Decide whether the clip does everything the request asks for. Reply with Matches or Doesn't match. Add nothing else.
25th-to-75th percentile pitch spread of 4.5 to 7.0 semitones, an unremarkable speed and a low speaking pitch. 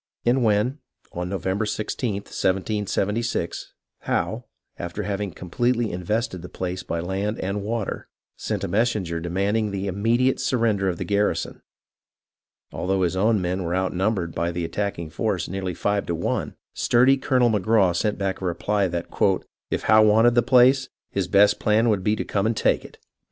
Doesn't match